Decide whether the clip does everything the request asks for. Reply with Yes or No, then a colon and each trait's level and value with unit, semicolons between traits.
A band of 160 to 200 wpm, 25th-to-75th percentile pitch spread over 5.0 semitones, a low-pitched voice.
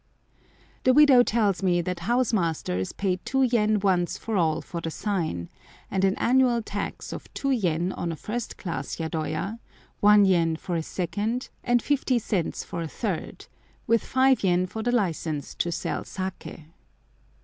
No: average, 165 wpm; wide, 5.5 semitones; high, 195 Hz